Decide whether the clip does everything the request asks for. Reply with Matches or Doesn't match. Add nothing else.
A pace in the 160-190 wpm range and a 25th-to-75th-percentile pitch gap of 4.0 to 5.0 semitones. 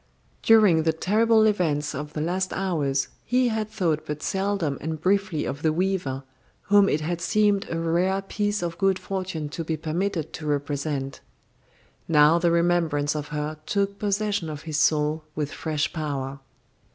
Matches